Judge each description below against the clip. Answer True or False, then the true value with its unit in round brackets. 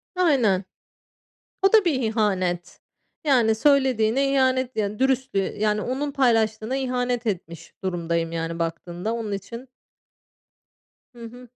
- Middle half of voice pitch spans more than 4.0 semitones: True (5.0 semitones)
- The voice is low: False (225 Hz)